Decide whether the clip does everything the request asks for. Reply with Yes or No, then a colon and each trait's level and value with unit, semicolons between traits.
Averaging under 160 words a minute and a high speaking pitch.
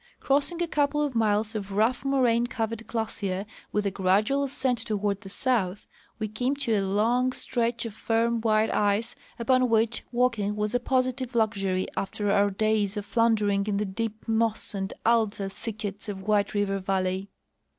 No: average, 170 wpm; high, 220 Hz